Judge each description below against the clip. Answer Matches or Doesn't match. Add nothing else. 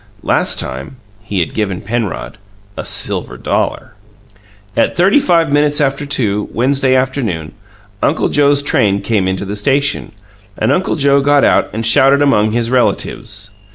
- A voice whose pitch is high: Doesn't match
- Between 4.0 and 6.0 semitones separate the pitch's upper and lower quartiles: Matches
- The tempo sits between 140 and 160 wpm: Matches